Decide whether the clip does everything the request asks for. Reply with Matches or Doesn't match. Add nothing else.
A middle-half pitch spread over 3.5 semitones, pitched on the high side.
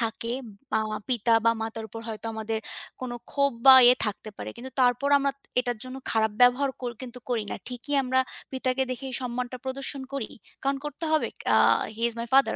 Doesn't match